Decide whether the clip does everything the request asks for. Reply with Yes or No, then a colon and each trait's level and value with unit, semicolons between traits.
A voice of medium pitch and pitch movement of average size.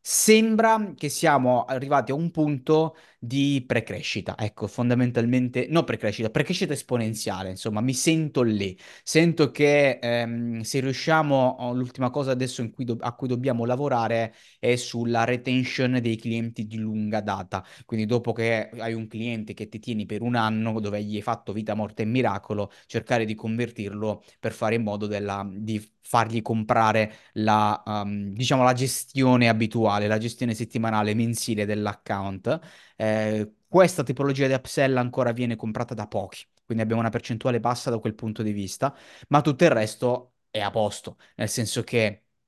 No: low, 115 Hz; average, 3.0 semitones